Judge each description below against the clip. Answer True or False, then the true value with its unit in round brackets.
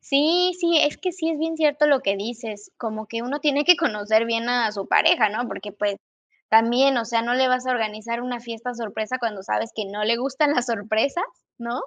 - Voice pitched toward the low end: False (240 Hz)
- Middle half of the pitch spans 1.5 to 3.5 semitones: False (4.5 semitones)